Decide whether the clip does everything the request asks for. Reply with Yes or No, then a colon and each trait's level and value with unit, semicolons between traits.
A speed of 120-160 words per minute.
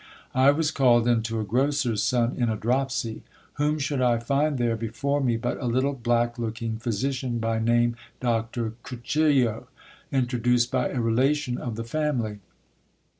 No: average, 170 wpm